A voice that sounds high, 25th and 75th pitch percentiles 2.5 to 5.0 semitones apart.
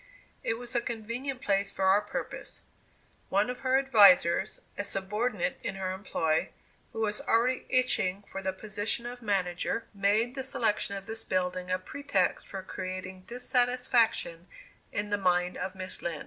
Yes: high, 205 Hz; average, 4.2 semitones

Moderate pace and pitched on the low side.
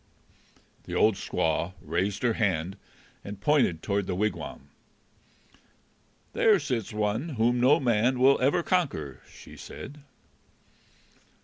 No: slow, 115 wpm; low, 110 Hz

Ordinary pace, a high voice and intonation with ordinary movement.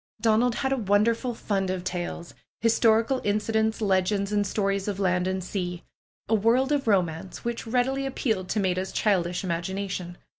Yes: average, 160 wpm; high, 205 Hz; average, 3.5 semitones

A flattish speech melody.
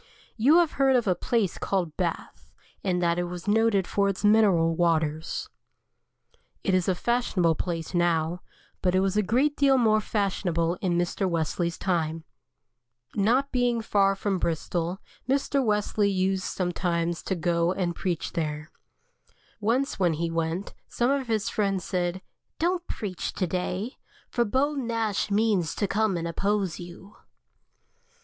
No: average, 4.2 semitones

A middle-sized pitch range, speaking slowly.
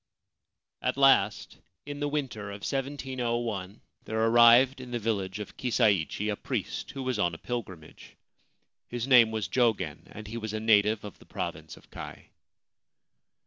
No: average, 3.6 semitones; average, 155 wpm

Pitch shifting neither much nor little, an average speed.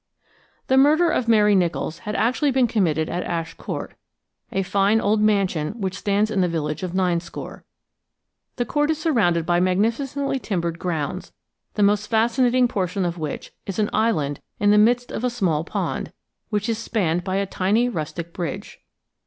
Yes: average, 4.9 semitones; average, 170 wpm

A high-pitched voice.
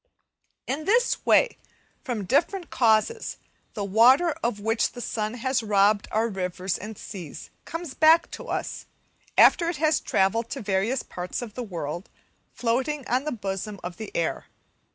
Yes: high, 230 Hz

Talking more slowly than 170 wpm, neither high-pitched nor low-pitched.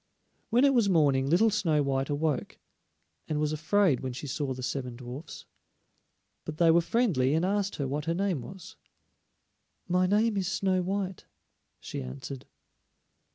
Yes: average, 155 wpm; medium, 160 Hz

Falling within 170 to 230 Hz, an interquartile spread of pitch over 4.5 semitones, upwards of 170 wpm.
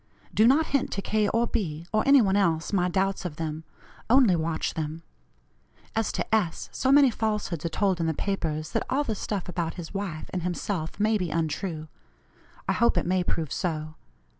Yes: medium, 185 Hz; average, 4.9 semitones; average, 195 wpm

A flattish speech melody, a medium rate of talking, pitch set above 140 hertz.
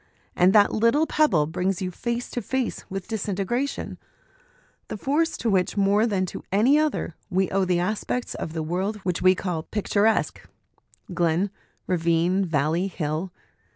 No: average, 4.0 semitones; average, 155 wpm; high, 190 Hz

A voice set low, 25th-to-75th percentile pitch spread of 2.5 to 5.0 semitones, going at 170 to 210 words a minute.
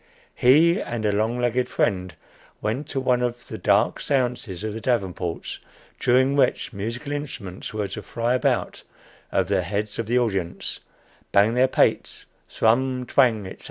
No: low, 115 Hz; average, 3.7 semitones; average, 160 wpm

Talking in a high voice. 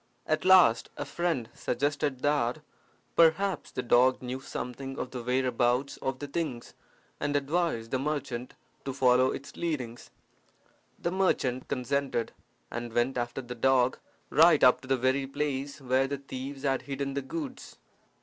No: low, 135 Hz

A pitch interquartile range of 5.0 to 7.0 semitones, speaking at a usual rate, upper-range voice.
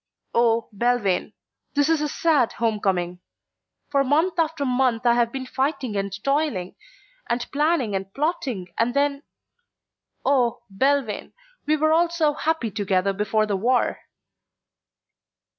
No: wide, 5.6 semitones; slow, 130 wpm; very high, 250 Hz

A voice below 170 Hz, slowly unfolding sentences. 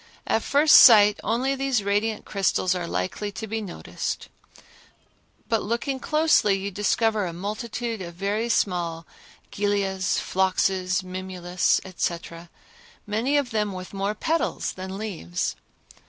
No: high, 200 Hz; slow, 125 wpm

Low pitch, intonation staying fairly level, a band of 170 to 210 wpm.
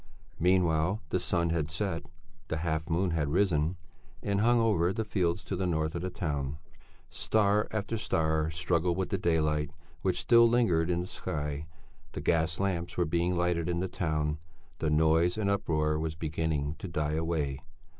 No: very low, 85 Hz; average, 3.0 semitones; average, 175 wpm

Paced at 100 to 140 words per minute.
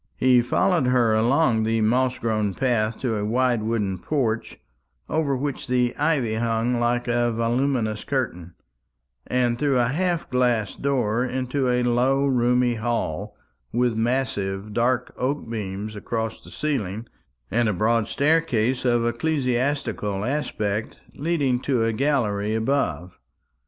Yes: slow, 135 wpm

